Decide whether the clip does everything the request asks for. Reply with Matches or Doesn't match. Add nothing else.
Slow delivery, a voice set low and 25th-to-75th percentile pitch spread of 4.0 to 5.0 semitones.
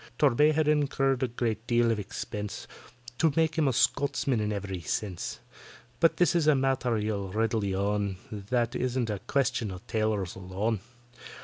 Doesn't match